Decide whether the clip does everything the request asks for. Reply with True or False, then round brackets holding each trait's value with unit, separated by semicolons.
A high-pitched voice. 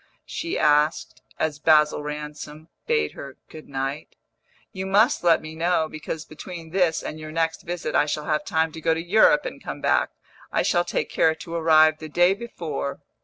False (160 Hz)